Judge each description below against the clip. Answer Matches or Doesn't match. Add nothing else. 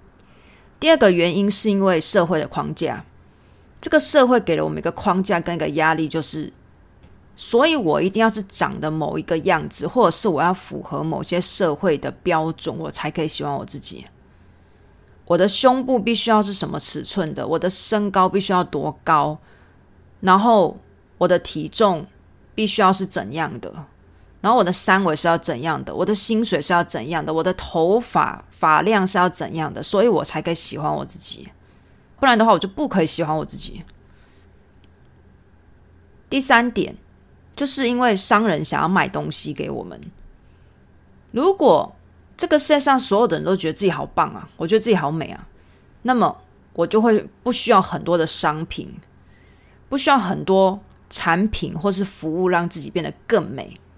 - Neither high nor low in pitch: Matches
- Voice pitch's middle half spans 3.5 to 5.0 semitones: Doesn't match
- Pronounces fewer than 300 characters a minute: Matches